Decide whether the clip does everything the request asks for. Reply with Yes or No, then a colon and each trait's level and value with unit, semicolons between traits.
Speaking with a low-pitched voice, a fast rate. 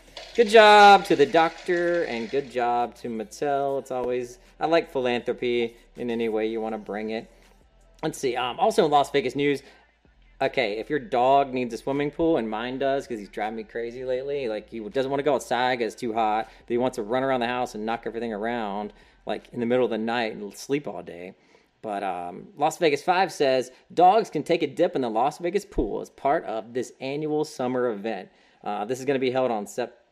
Yes: low, 130 Hz; fast, 225 wpm